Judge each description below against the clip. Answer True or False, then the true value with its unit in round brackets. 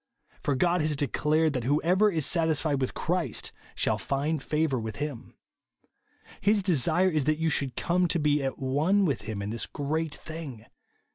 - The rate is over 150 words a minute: True (170 wpm)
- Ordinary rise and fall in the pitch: True (3.3 semitones)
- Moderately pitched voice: True (150 Hz)